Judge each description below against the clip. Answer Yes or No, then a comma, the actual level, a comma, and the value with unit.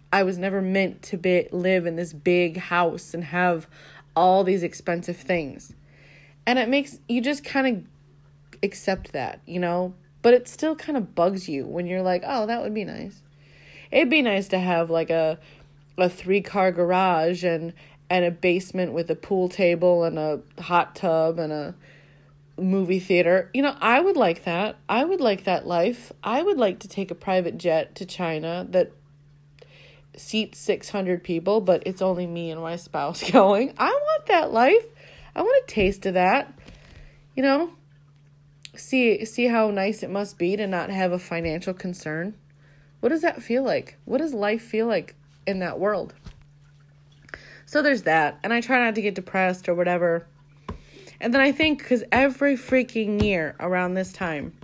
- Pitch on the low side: No, medium, 180 Hz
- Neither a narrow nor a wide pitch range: Yes, average, 4.7 semitones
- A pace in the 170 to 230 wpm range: Yes, average, 180 wpm